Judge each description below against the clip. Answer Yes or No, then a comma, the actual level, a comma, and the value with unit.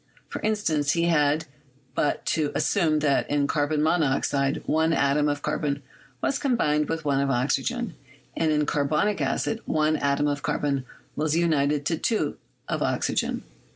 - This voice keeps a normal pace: Yes, average, 155 wpm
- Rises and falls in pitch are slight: Yes, narrow, 2.3 semitones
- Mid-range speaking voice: Yes, medium, 150 Hz